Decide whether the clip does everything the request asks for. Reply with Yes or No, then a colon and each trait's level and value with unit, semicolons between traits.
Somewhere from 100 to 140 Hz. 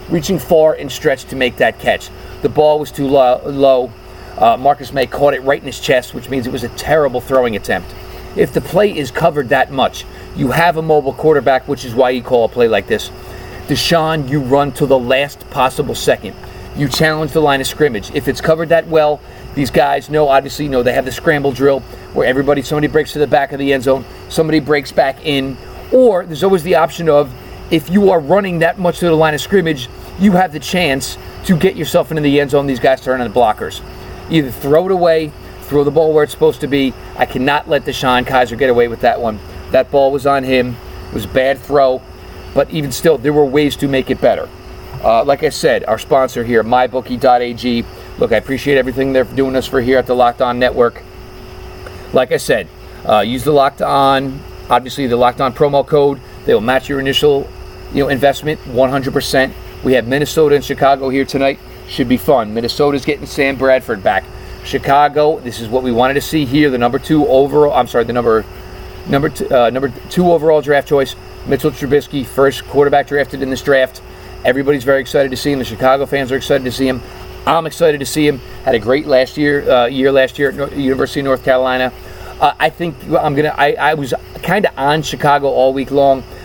Yes: low, 135 Hz